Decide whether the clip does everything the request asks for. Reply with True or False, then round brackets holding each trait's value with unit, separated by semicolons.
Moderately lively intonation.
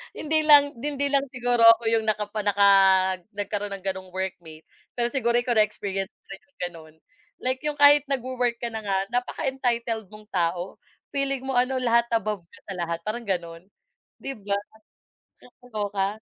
True (4.6 semitones)